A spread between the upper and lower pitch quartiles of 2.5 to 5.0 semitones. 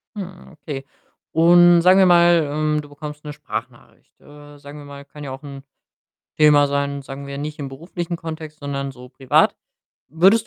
Yes: average, 2.9 semitones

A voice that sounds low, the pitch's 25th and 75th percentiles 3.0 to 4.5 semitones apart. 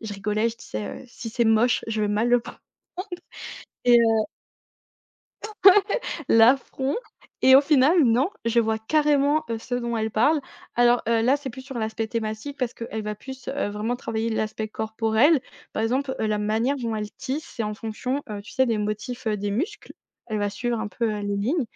No: high, 230 Hz; average, 3.3 semitones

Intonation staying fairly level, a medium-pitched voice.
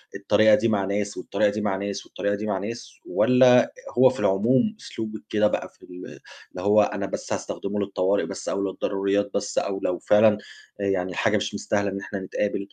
No: narrow, 1.5 semitones; low, 100 Hz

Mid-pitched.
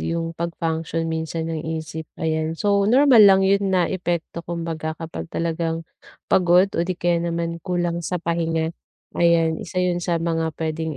Yes: medium, 170 Hz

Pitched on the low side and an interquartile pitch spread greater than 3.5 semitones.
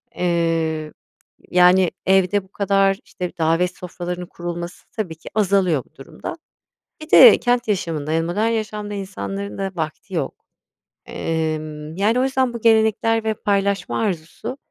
No: high, 190 Hz; average, 4.3 semitones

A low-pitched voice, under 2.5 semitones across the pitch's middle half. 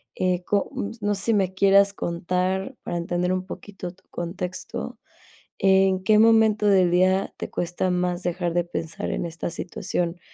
No: medium, 185 Hz; narrow, 2.1 semitones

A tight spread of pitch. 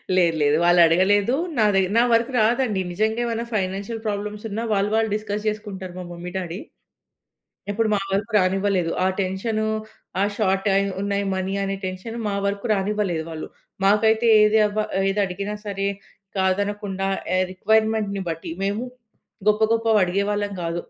Yes: narrow, 2.3 semitones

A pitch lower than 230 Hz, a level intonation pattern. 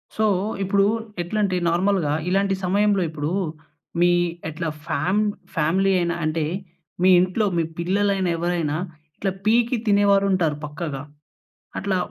No: medium, 185 Hz; average, 3.1 semitones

